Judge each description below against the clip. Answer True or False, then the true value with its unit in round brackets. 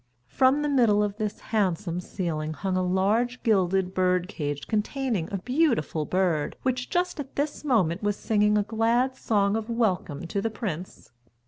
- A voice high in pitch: True (205 Hz)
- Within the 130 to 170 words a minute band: True (165 wpm)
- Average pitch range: True (4.7 semitones)